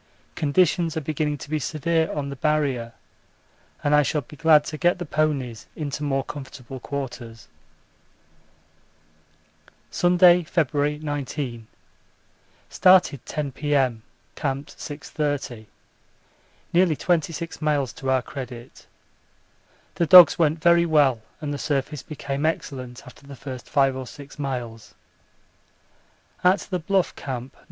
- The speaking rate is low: Yes, slow, 125 wpm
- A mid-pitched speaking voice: Yes, medium, 145 Hz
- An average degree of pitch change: Yes, average, 3.0 semitones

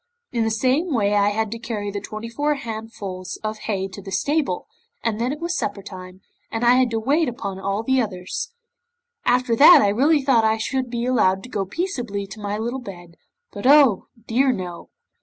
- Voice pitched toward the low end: No, high, 225 Hz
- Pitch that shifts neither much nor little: Yes, average, 4.2 semitones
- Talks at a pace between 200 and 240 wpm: Yes, fast, 205 wpm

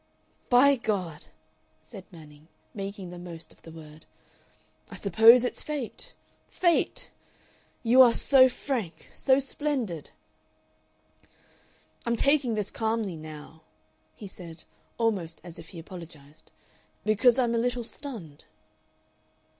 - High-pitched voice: Yes, high, 210 Hz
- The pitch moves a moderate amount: No, wide, 6.9 semitones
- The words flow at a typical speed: No, slow, 115 wpm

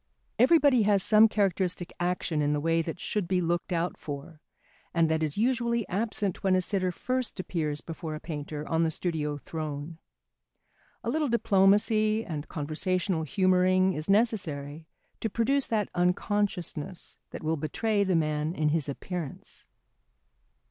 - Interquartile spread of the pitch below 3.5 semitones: No, average, 4.7 semitones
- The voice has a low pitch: No, medium, 180 Hz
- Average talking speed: Yes, average, 150 wpm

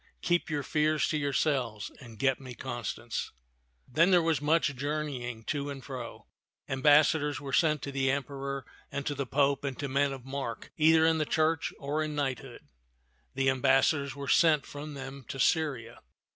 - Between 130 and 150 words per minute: No, average, 180 wpm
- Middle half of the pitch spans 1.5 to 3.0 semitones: Yes, narrow, 2.4 semitones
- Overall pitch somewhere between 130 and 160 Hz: Yes, medium, 140 Hz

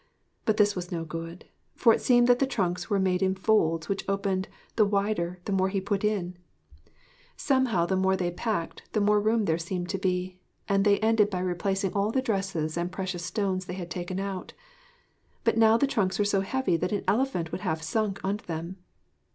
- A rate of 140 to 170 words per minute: No, fast, 205 wpm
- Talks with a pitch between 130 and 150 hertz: No, high, 190 Hz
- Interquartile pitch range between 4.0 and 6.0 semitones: No, average, 2.8 semitones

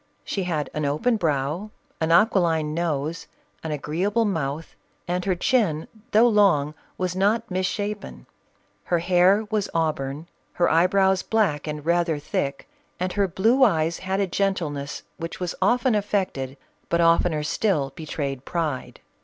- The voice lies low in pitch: No, medium, 170 Hz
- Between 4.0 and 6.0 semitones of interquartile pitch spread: Yes, average, 4.6 semitones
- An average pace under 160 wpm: Yes, average, 145 wpm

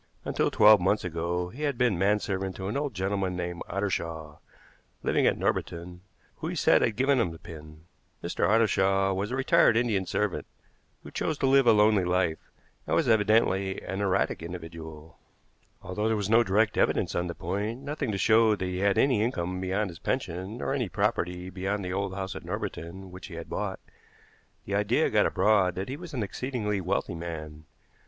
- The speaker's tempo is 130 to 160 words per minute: No, average, 190 wpm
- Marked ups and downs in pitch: No, average, 3.6 semitones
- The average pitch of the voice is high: No, very low, 95 Hz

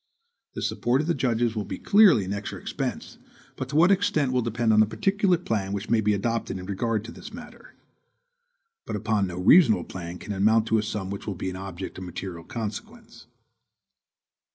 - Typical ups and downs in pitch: Yes, average, 4.5 semitones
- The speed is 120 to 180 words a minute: No, average, 200 wpm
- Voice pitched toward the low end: Yes, low, 110 Hz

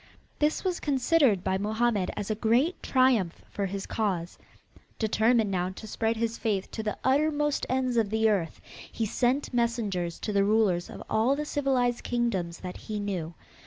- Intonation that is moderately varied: Yes, average, 4.1 semitones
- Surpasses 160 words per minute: Yes, average, 170 wpm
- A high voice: Yes, high, 220 Hz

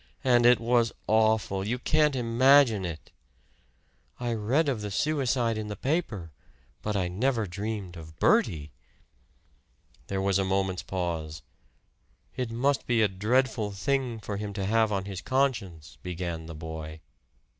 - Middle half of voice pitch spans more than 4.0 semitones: Yes, average, 4.8 semitones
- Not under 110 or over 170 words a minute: Yes, average, 145 wpm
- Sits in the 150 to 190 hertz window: No, low, 105 Hz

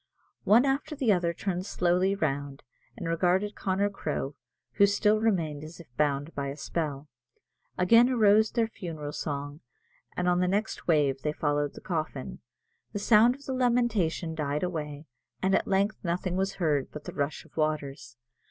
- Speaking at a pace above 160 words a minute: Yes, average, 170 wpm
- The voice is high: No, medium, 175 Hz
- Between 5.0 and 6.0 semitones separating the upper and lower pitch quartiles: Yes, wide, 5.4 semitones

